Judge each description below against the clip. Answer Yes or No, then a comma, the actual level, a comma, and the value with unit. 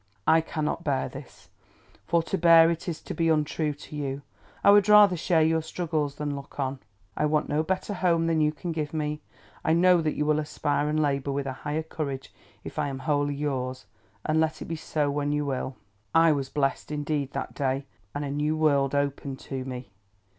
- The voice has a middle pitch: Yes, medium, 150 Hz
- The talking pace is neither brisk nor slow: No, fast, 210 wpm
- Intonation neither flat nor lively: No, narrow, 2.2 semitones